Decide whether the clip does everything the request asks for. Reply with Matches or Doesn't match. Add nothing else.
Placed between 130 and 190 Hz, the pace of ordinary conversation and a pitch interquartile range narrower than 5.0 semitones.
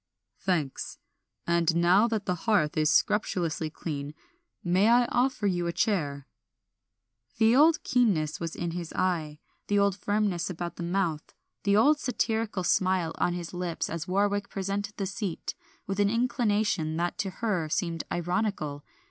Matches